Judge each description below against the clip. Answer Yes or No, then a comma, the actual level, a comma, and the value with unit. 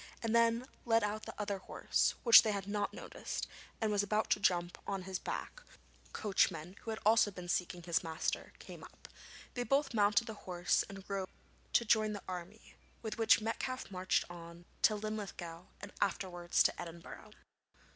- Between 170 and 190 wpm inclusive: Yes, average, 180 wpm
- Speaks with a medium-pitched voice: No, high, 205 Hz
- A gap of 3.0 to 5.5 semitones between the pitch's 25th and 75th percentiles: Yes, average, 3.5 semitones